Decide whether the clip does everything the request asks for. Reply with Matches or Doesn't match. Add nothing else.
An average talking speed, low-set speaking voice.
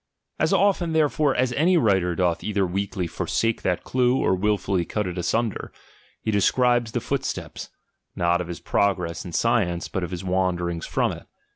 Matches